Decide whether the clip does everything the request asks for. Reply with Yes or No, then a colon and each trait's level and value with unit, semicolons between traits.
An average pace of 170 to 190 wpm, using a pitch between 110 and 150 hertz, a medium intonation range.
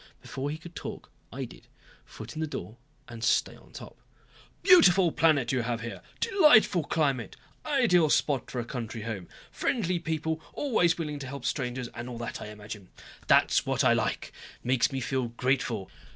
No: average, 175 wpm; low, 135 Hz; wide, 5.7 semitones